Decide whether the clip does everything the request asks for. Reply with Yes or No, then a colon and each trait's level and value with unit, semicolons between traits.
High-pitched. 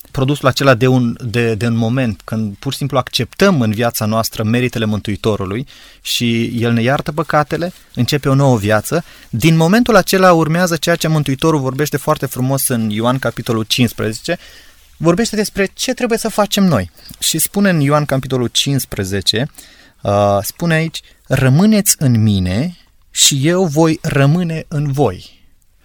No: low, 135 Hz